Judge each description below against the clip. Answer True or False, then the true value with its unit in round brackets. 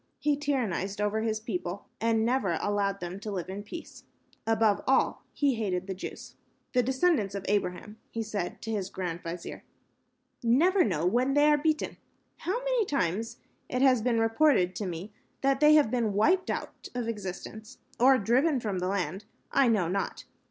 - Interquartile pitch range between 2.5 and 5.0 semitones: False (5.4 semitones)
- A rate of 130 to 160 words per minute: False (175 wpm)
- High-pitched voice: True (220 Hz)